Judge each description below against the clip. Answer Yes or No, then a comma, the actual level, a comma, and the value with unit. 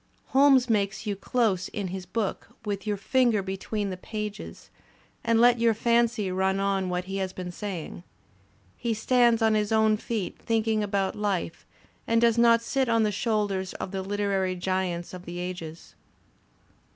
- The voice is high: Yes, high, 205 Hz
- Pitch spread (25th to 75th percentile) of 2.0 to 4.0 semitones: Yes, average, 3.2 semitones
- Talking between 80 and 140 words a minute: No, average, 165 wpm